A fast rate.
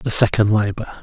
No: average, 175 wpm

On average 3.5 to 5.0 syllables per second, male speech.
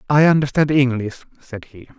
No: 5.4 syllables/s; male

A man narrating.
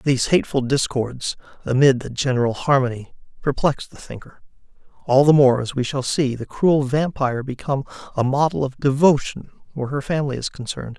Yes: male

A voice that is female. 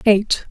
Yes: female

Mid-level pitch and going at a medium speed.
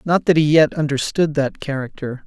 Yes: medium, 145 Hz; average, 185 wpm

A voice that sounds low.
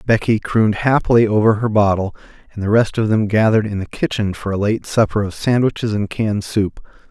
Yes: low, 105 Hz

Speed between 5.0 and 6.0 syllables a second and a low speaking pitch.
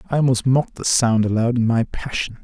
Yes: 5.7 syllables/s; low, 120 Hz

